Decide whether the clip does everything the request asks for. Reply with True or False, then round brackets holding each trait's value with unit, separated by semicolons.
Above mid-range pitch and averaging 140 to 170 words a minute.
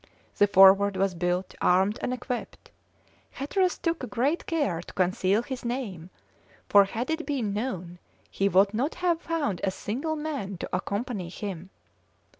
True (205 Hz; 150 wpm)